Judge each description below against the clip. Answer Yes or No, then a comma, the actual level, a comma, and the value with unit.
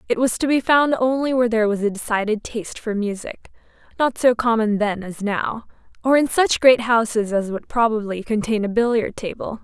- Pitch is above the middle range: Yes, high, 225 Hz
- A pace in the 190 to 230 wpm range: Yes, average, 200 wpm